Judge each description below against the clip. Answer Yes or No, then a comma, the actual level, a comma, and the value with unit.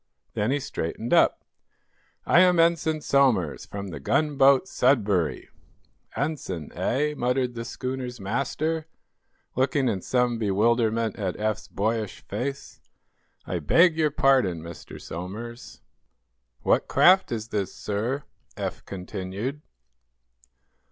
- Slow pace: Yes, slow, 110 wpm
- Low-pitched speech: Yes, low, 120 Hz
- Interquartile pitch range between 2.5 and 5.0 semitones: No, wide, 5.5 semitones